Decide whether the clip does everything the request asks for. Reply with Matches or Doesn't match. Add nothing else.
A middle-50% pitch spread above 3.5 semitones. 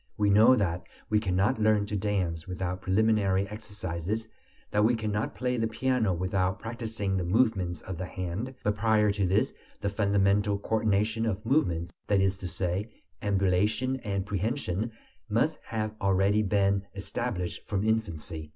Doesn't match